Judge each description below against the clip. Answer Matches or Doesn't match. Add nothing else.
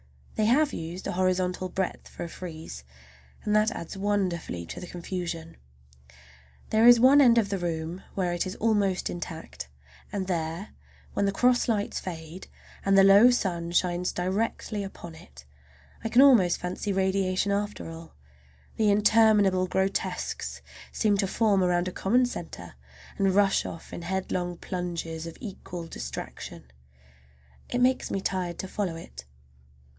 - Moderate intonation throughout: Matches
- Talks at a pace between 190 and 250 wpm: Doesn't match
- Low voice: Doesn't match